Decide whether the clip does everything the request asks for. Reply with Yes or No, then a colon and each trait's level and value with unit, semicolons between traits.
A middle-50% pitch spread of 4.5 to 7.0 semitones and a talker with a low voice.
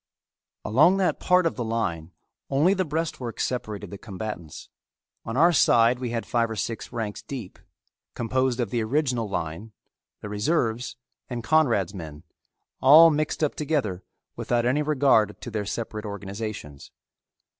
Yes: average, 5.1 semitones; low, 115 Hz